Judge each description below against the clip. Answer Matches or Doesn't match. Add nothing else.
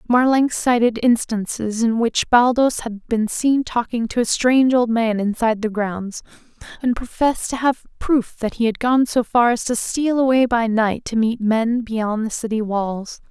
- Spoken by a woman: Matches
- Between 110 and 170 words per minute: Doesn't match